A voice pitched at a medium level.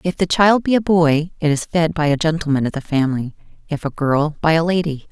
Yes: medium, 160 Hz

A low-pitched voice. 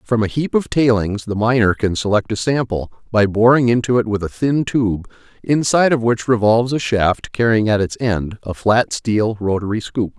Yes: low, 110 Hz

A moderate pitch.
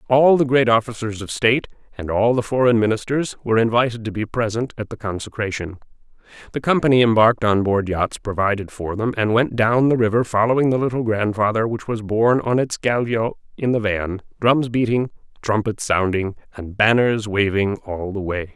No: low, 110 Hz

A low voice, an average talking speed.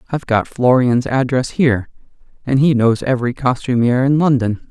Yes: low, 125 Hz; average, 155 wpm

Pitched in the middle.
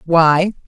Yes: medium, 170 Hz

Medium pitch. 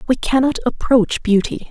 No: high, 245 Hz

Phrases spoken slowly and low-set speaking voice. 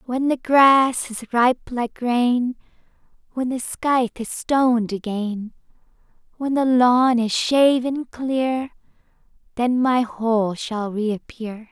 No: slow, 125 wpm; high, 245 Hz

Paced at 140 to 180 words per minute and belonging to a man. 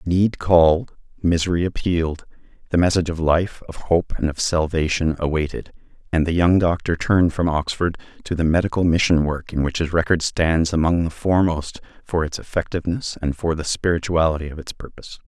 Yes: average, 170 wpm; male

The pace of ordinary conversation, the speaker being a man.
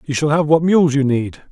No: fast, 275 wpm; male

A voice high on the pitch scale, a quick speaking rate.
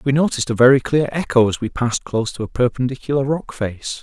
No: low, 130 Hz; fast, 225 wpm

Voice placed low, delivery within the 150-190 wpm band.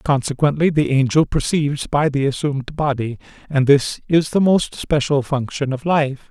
No: medium, 145 Hz; average, 160 wpm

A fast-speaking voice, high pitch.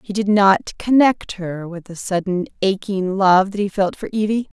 No: average, 195 wpm; high, 195 Hz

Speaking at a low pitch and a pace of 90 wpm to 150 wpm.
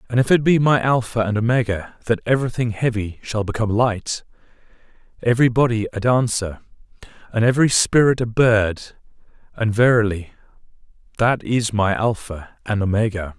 Yes: low, 110 Hz; average, 140 wpm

